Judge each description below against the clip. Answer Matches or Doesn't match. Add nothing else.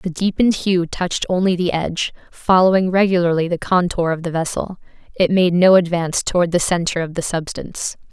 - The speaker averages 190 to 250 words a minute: Doesn't match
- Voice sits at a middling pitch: Matches